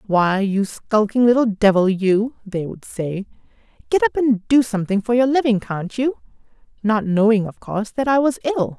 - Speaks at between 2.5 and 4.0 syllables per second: No, 4.8 syllables/s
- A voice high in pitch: Yes, high, 220 Hz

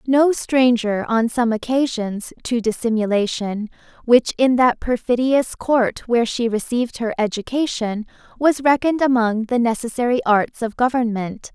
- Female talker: Yes, female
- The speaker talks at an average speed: No, slow, 130 wpm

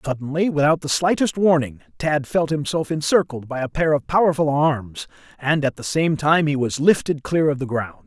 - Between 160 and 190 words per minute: No, average, 200 wpm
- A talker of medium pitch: Yes, medium, 150 Hz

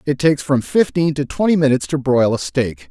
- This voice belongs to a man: Yes, male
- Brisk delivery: Yes, fast, 225 wpm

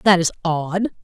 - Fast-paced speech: No, average, 175 wpm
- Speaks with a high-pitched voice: No, medium, 180 Hz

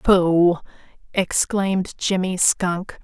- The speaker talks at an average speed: No, slow, 80 wpm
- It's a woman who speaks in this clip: Yes, female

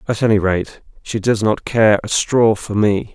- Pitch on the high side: No, low, 110 Hz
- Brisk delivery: Yes, fast, 210 wpm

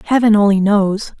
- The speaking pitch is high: Yes, high, 205 Hz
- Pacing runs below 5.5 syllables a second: Yes, 4.8 syllables/s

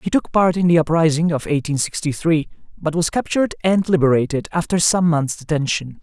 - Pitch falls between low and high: Yes, medium, 160 Hz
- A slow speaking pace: No, average, 190 wpm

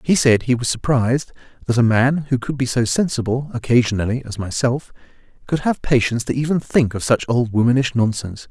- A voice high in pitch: No, low, 125 Hz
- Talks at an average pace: Yes, average, 190 wpm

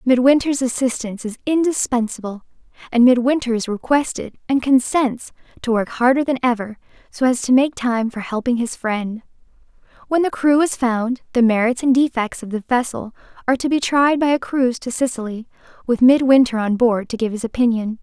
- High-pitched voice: Yes, high, 245 Hz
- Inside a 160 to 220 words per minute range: Yes, average, 175 wpm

